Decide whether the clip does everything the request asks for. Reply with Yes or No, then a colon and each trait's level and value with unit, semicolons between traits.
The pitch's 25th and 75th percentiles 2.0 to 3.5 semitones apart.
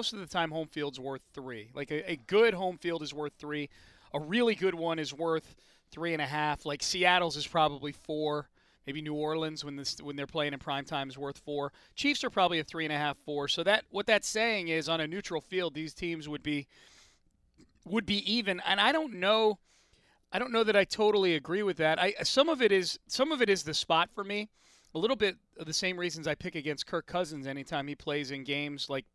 No: average, 4.9 semitones